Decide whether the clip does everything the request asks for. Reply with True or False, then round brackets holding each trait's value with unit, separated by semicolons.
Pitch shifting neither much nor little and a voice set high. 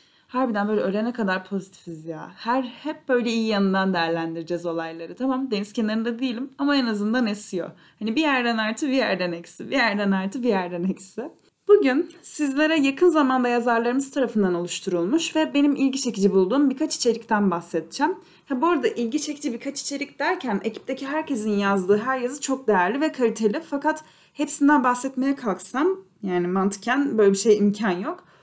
False (6.0 semitones; 235 Hz)